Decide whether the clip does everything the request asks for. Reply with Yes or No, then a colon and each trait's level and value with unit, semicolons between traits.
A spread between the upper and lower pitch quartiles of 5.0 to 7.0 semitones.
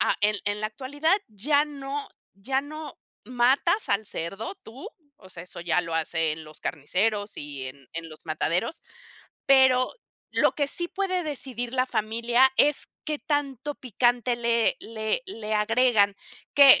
Yes: wide, 5.6 semitones